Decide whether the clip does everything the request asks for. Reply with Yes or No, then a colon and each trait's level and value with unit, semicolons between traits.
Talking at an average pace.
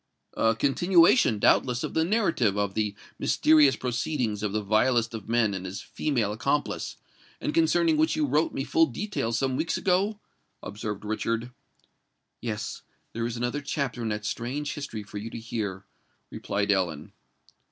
Yes: average, 155 wpm